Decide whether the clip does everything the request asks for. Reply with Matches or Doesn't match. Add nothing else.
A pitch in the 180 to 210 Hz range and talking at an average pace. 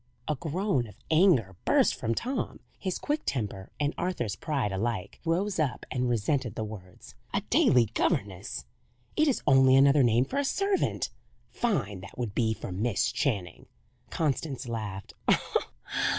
Doesn't match